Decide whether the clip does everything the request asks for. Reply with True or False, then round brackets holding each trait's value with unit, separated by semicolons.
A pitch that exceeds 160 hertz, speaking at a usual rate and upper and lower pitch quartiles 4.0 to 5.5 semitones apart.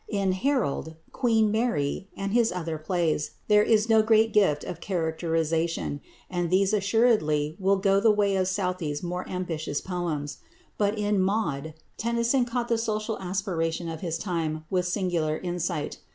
True (185 Hz; 150 wpm; 4.6 semitones)